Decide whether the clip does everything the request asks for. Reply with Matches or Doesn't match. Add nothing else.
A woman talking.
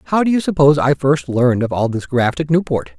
Doesn't match